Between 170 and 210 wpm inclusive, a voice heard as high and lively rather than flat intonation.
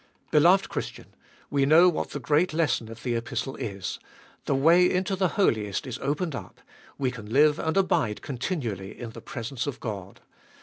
No: average, 175 wpm; low, 135 Hz; wide, 6.3 semitones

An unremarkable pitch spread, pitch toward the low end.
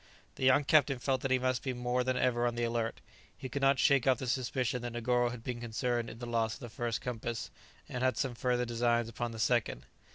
No: narrow, 1.5 semitones; low, 120 Hz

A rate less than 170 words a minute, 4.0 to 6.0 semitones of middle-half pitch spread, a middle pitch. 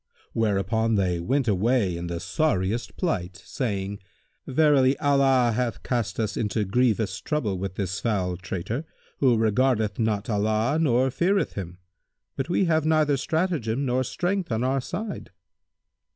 No: average, 140 wpm; wide, 5.5 semitones; low, 115 Hz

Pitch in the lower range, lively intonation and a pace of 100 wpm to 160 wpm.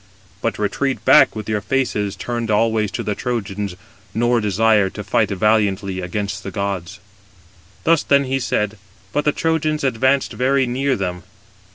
No: low, 110 Hz; average, 4.7 semitones; average, 155 wpm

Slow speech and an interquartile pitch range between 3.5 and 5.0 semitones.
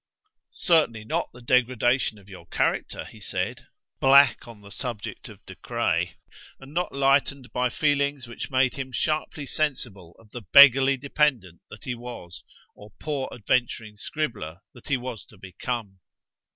No: average, 150 wpm; average, 4.5 semitones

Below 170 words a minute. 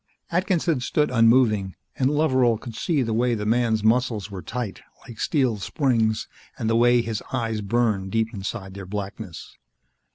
Yes: average, 160 wpm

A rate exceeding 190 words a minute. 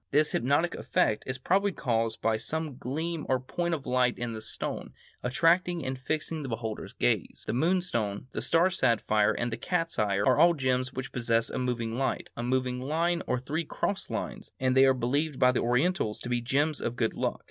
Yes: average, 200 wpm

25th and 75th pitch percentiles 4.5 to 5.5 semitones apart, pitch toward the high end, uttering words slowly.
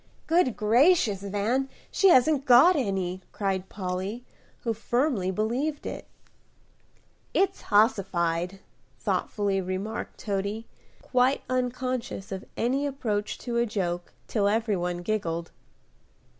Yes: average, 4.8 semitones; high, 215 Hz; slow, 110 wpm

